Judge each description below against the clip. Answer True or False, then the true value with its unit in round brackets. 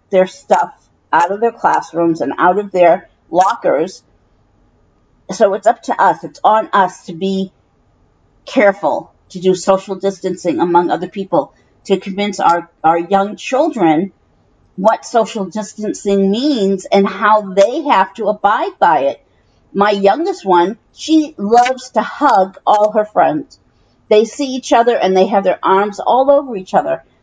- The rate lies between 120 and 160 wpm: True (155 wpm)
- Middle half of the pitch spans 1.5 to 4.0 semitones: True (3.0 semitones)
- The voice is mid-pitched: False (195 Hz)